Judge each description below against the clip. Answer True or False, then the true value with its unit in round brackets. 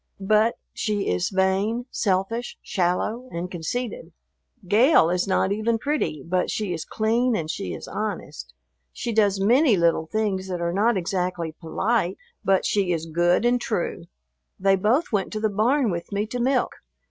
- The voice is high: True (200 Hz)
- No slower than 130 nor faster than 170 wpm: True (165 wpm)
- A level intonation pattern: False (4.3 semitones)